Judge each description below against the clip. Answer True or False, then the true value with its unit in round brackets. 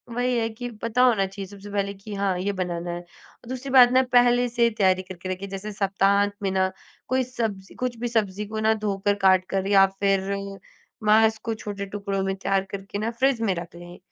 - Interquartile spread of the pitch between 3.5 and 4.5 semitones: False (2.8 semitones)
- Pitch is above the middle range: True (200 Hz)